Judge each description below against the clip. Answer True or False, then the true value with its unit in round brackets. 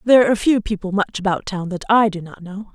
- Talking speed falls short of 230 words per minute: False (260 wpm)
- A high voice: True (200 Hz)